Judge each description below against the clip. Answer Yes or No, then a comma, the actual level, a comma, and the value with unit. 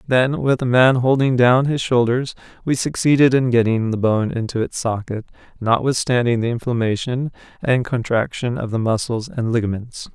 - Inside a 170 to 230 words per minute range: No, average, 160 wpm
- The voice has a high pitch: No, low, 120 Hz